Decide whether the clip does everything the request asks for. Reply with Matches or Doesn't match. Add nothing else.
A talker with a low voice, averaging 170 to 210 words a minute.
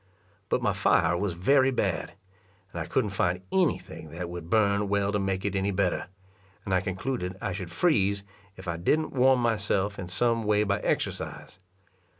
Matches